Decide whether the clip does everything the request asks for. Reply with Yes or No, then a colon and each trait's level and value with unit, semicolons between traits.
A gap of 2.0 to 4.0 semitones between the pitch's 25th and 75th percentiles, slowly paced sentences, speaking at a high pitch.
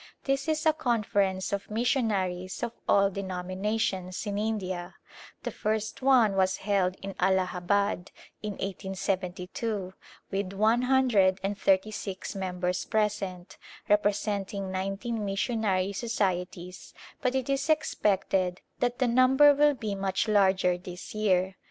Yes: average, 3.0 semitones; slow, 125 wpm; high, 200 Hz